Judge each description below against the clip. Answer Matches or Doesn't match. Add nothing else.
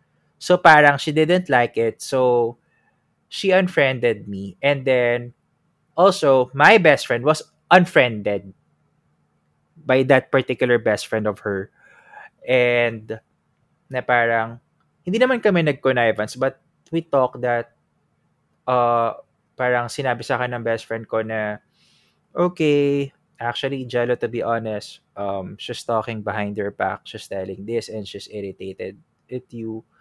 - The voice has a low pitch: Matches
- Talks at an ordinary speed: Matches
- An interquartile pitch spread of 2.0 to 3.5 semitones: Doesn't match